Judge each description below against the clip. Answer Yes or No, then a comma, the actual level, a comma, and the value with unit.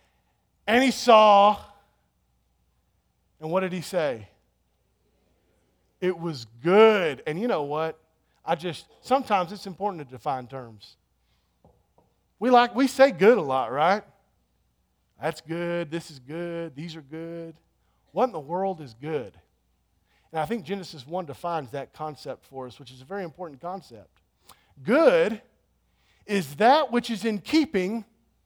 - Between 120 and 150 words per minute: Yes, average, 145 wpm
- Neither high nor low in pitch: Yes, medium, 165 Hz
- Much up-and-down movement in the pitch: Yes, wide, 8.2 semitones